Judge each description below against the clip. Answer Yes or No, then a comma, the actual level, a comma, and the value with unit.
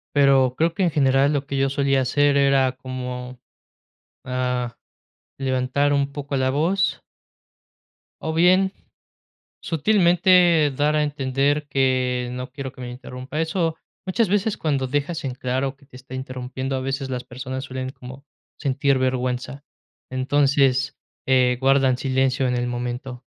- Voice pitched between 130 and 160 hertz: Yes, low, 135 Hz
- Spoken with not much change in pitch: Yes, narrow, 2.0 semitones